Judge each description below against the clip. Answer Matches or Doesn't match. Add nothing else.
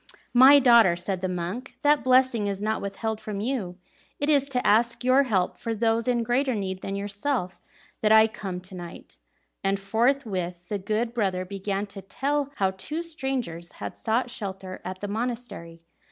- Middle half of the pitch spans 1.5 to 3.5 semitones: Doesn't match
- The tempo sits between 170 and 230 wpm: Matches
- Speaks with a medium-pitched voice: Doesn't match